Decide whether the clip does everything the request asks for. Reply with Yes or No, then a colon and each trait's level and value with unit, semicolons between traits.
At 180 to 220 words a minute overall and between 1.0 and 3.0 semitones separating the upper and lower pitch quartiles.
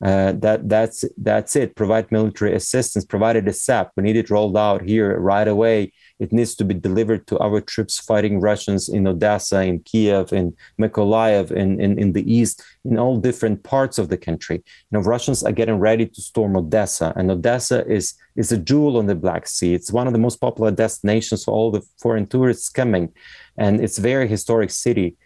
Yes: average, 200 wpm; narrow, 2.4 semitones